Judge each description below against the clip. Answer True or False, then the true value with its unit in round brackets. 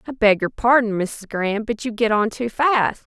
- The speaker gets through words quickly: True (210 wpm)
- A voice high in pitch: True (225 Hz)